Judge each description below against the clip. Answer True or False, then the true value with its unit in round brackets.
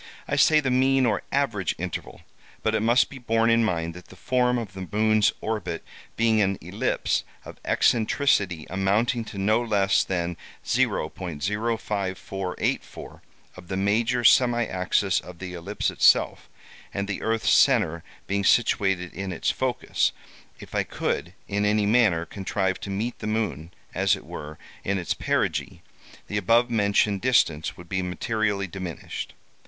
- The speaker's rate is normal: True (150 wpm)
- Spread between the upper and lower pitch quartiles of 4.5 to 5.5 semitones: False (3.7 semitones)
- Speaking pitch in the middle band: False (100 Hz)